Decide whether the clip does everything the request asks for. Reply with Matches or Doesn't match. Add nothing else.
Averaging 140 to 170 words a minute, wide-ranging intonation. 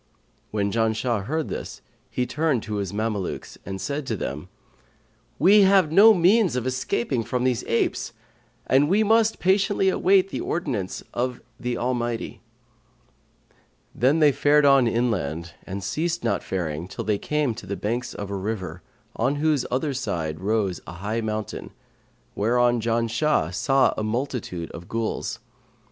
Matches